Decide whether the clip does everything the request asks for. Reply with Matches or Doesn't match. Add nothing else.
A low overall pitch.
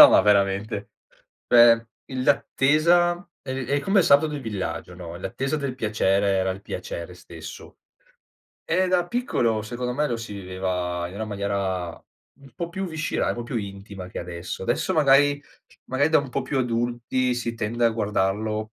Matches